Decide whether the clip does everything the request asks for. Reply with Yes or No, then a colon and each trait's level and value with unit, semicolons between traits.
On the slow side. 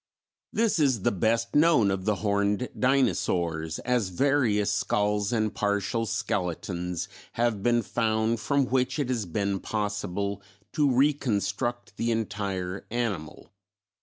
Yes: slow, 125 wpm